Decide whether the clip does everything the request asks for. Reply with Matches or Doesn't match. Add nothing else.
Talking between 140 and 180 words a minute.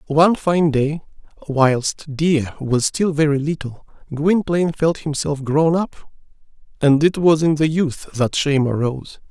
Matches